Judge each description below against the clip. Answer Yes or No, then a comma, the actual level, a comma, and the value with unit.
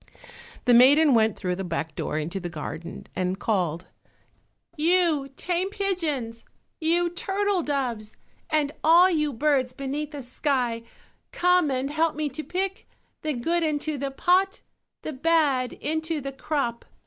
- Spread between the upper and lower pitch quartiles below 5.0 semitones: No, wide, 5.5 semitones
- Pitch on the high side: Yes, very high, 290 Hz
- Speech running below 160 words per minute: Yes, average, 145 wpm